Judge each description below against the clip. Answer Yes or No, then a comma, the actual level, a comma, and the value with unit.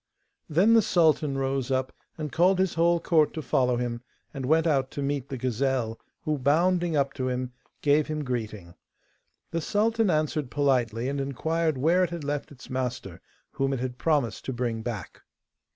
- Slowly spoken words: No, average, 180 wpm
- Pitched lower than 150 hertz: Yes, medium, 140 Hz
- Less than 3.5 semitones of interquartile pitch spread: No, average, 4.1 semitones